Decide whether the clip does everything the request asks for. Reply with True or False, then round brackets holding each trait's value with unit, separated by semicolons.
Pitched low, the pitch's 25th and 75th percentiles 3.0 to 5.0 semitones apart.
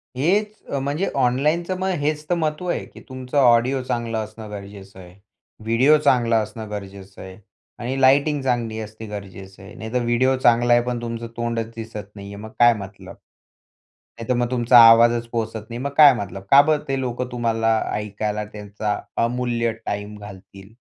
True (115 Hz; 3.6 semitones)